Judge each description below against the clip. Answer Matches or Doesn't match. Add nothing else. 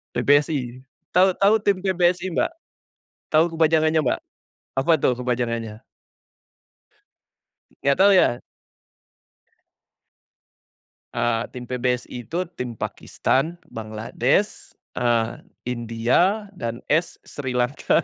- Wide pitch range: Matches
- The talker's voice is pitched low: Matches